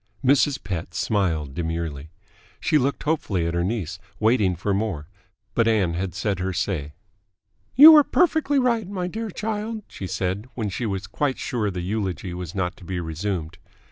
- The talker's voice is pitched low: Yes, low, 100 Hz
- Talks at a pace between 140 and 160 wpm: No, average, 170 wpm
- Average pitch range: No, wide, 7.5 semitones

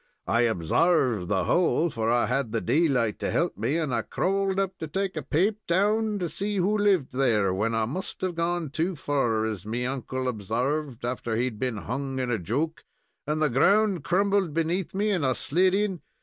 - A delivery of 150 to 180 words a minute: No, fast, 205 wpm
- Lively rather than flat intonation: Yes, wide, 7.4 semitones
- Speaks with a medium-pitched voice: Yes, medium, 145 Hz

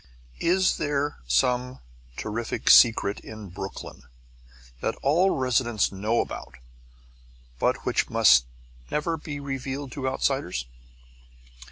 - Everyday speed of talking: No, slow, 100 wpm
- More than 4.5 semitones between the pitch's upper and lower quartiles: Yes, average, 5.3 semitones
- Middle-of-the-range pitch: No, low, 125 Hz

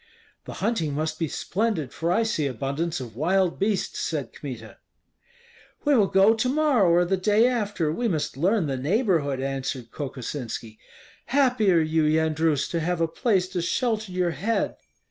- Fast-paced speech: No, average, 165 wpm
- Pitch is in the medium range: Yes, medium, 170 Hz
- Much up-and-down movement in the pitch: Yes, wide, 6.0 semitones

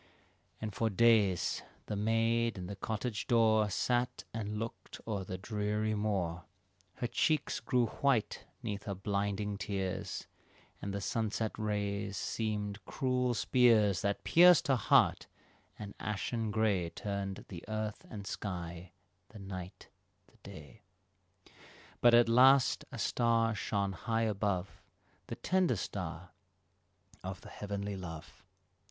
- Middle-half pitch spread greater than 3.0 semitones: No, narrow, 2.6 semitones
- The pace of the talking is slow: Yes, slow, 130 wpm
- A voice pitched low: Yes, low, 105 Hz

